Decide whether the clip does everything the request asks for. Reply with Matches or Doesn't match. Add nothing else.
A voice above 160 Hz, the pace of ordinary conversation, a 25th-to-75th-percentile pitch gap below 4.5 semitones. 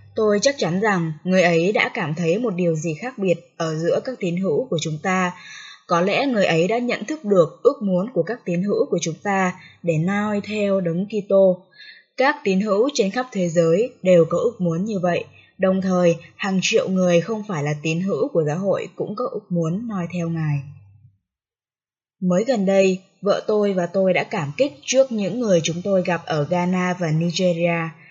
Matches